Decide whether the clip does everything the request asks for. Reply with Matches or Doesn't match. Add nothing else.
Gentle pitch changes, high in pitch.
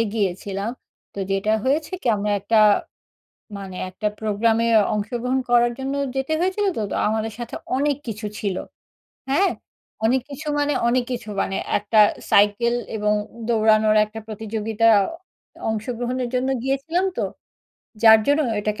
Doesn't match